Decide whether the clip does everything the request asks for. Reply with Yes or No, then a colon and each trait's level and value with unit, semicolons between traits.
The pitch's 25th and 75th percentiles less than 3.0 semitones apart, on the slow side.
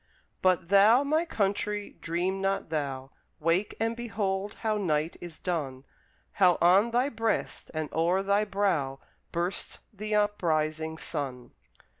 No: average, 4.6 semitones; slow, 130 wpm